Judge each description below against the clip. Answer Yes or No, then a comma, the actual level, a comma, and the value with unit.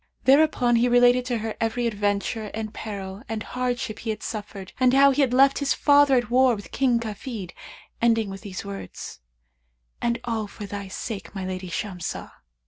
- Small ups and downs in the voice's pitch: No, average, 3.5 semitones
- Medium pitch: No, high, 225 Hz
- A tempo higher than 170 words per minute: Yes, average, 180 wpm